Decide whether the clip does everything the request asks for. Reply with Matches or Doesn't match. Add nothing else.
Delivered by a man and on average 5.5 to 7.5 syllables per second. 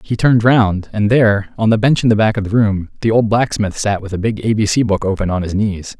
Matches